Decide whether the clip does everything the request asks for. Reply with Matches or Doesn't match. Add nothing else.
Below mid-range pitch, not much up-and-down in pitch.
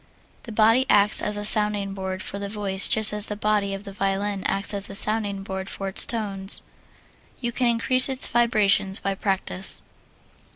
Doesn't match